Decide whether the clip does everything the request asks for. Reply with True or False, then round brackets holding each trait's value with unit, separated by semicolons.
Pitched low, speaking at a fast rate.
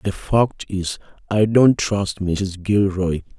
False (100 Hz; 140 wpm)